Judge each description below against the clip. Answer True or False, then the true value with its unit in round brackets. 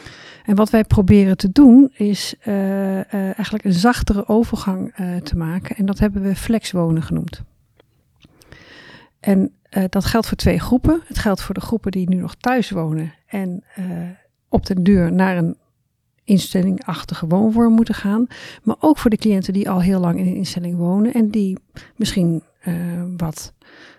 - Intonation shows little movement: False (3.3 semitones)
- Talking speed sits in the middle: True (175 wpm)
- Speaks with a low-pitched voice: False (195 Hz)